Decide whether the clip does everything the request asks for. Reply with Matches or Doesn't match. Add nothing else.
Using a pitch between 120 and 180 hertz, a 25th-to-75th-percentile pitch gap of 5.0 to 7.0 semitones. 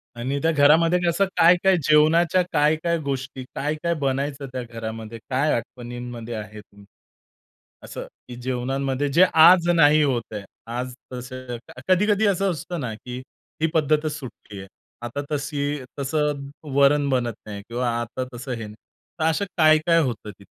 Doesn't match